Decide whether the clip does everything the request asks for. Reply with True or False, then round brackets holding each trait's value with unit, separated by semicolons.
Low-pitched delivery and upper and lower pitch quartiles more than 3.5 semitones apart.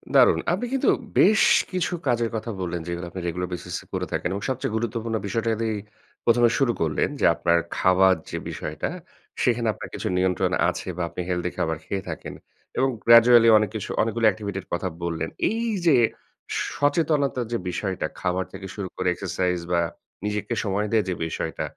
True (105 Hz; 4.4 semitones)